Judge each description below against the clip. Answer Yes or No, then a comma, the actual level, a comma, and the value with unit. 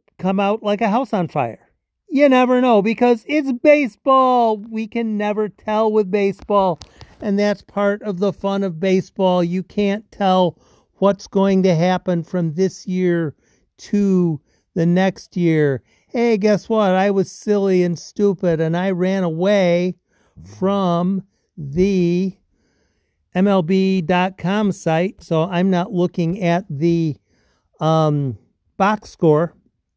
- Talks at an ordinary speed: No, slow, 130 wpm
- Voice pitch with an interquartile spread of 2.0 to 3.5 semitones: Yes, average, 3.1 semitones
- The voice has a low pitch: No, high, 190 Hz